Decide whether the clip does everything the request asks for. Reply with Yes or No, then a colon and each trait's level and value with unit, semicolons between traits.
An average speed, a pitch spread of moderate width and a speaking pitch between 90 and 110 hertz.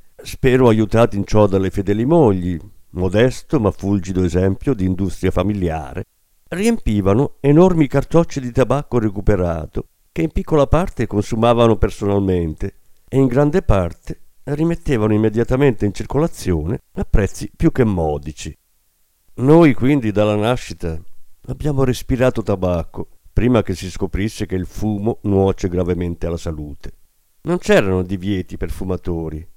No: average, 125 wpm; wide, 5.8 semitones; low, 105 Hz